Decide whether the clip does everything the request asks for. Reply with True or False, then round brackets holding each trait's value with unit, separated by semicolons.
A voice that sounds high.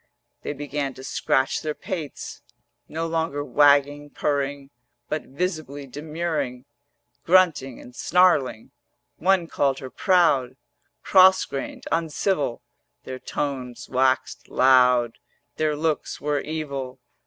False (145 Hz)